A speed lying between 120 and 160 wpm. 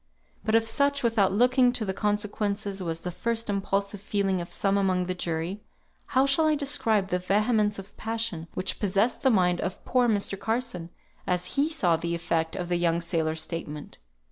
No: average, 185 wpm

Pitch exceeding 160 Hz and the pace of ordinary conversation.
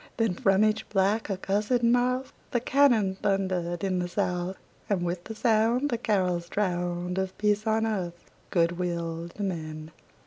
Yes: high, 190 Hz; average, 160 wpm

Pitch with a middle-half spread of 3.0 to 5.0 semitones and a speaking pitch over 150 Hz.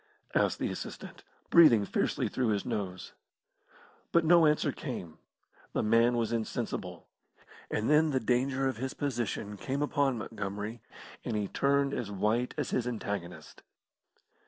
No: average, 4.7 semitones; low, 120 Hz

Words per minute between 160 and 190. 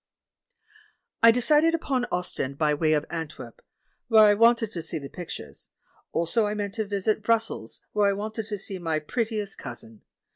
Yes: average, 175 wpm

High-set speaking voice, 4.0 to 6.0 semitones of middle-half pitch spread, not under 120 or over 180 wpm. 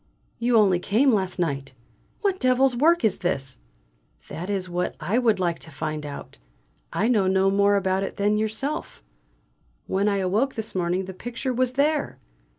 Yes: high, 200 Hz; average, 5.0 semitones; average, 175 wpm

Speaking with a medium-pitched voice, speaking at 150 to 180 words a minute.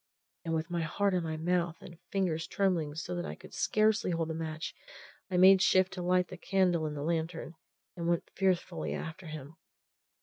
No: medium, 170 Hz; average, 195 wpm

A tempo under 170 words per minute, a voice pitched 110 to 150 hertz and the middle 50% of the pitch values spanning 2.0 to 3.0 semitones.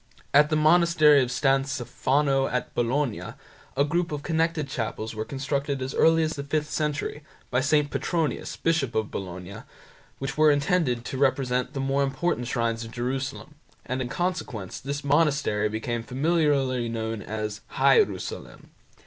No: average, 150 wpm; low, 135 Hz; average, 3.7 semitones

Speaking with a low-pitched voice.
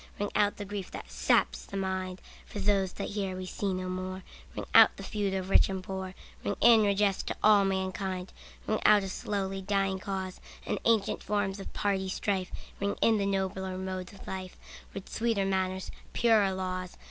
No: high, 190 Hz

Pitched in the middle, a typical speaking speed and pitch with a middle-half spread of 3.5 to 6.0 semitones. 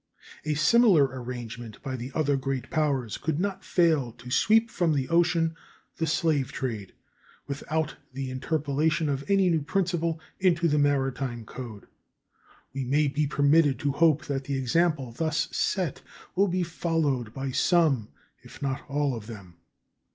Yes: medium, 145 Hz; average, 150 wpm; average, 3.9 semitones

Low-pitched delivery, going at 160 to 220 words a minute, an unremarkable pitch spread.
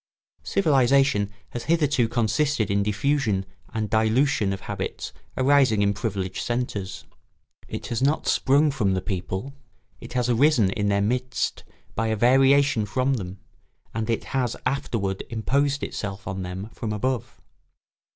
No: low, 115 Hz; average, 140 wpm; average, 5.0 semitones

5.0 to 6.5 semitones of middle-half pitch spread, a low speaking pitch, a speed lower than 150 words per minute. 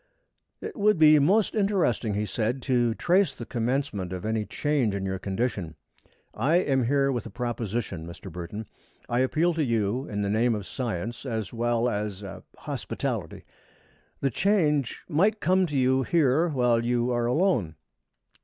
No: wide, 5.6 semitones; low, 120 Hz; average, 165 wpm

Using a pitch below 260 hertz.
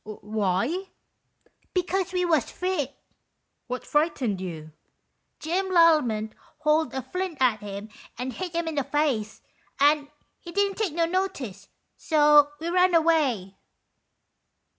No: very high, 300 Hz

